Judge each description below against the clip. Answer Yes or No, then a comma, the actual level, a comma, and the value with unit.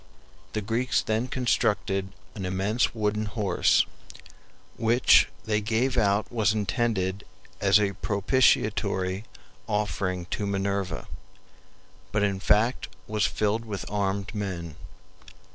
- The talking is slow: Yes, slow, 110 wpm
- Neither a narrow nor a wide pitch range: No, narrow, 2.1 semitones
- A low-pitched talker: Yes, low, 105 Hz